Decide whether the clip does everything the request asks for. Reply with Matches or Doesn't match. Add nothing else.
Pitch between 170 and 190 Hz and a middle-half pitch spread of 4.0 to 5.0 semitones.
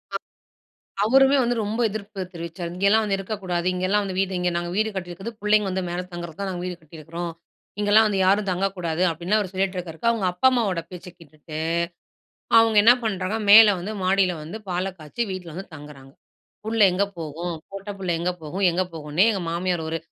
Doesn't match